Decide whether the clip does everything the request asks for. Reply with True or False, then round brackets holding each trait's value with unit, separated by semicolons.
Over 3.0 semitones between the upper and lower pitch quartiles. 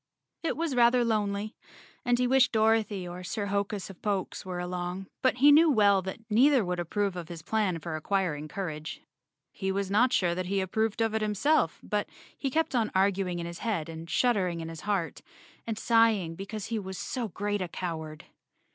True (4.0 semitones)